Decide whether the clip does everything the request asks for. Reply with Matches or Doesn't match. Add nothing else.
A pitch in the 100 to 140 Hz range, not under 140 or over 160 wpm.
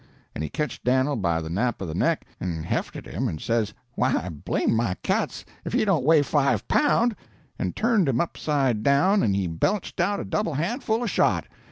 Doesn't match